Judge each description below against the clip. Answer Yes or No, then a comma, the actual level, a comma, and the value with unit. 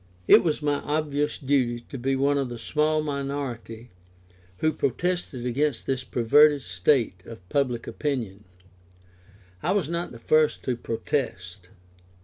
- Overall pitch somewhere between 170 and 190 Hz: No, low, 135 Hz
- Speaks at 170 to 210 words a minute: No, slow, 135 wpm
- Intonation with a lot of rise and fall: No, average, 4.0 semitones